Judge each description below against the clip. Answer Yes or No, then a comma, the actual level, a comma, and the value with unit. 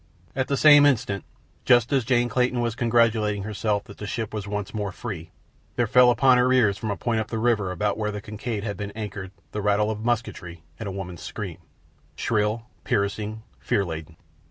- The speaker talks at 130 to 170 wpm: No, average, 195 wpm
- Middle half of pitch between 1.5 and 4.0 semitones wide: Yes, average, 2.9 semitones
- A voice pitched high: No, low, 105 Hz